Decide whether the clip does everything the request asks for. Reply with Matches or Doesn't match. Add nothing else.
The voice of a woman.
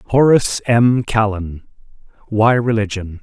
Doesn't match